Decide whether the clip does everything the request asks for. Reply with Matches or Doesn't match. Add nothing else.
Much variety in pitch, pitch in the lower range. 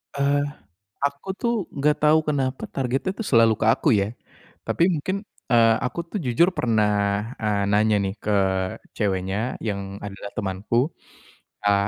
Matches